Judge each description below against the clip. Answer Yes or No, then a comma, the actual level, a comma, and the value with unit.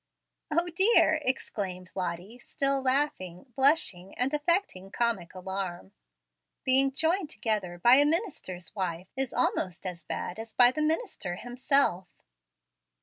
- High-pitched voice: Yes, high, 240 Hz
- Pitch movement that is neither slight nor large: No, wide, 7.7 semitones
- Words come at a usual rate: No, slow, 125 wpm